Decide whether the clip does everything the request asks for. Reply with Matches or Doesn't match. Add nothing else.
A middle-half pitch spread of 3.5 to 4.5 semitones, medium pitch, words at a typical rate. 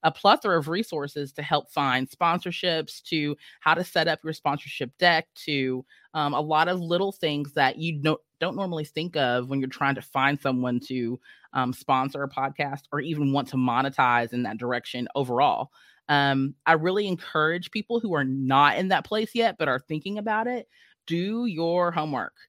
Matches